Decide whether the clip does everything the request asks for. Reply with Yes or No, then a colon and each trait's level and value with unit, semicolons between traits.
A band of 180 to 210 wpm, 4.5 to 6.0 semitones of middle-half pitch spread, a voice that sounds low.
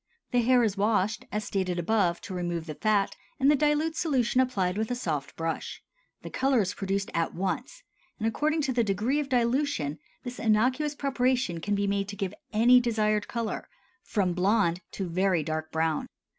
No: average, 185 wpm; wide, 5.5 semitones; high, 215 Hz